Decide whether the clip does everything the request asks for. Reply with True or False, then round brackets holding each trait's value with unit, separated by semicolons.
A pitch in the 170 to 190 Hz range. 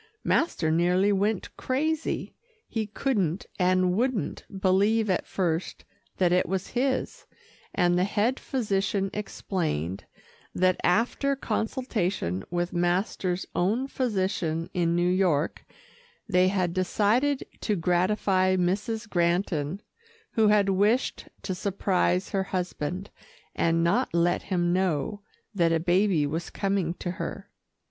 True (185 Hz)